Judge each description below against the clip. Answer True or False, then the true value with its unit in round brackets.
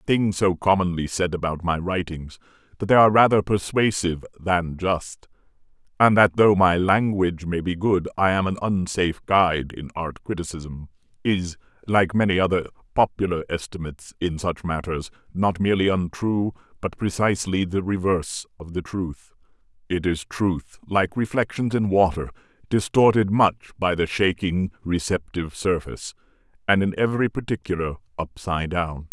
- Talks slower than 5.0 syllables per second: False (5.1 syllables/s)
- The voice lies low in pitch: True (90 Hz)